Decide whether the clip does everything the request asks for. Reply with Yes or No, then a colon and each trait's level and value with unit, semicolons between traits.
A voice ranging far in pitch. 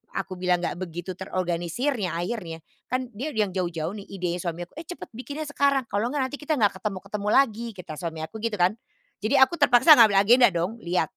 Yes: wide, 5.9 semitones